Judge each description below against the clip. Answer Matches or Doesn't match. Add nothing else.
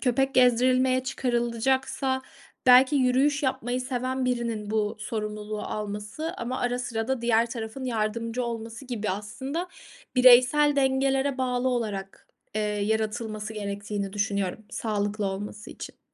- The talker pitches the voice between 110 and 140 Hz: Doesn't match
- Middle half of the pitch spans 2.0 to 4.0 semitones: Matches